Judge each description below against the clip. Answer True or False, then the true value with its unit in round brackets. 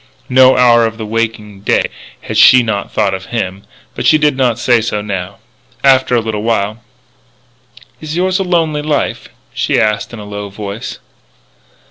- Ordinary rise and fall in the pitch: True (4.1 semitones)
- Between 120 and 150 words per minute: False (175 wpm)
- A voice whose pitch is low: True (115 Hz)